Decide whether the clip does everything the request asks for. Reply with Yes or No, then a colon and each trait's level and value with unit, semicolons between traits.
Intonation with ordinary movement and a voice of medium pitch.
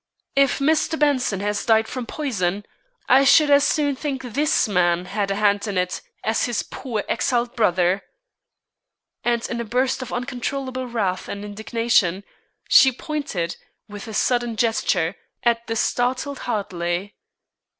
No: average, 4.4 semitones; high, 230 Hz